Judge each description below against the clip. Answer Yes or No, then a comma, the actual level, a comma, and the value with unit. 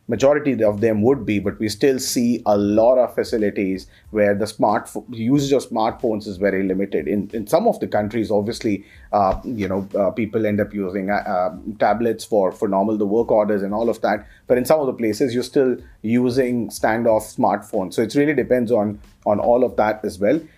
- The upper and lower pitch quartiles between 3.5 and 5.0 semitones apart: No, average, 2.9 semitones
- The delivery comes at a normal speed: No, fast, 210 wpm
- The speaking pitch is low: Yes, low, 110 Hz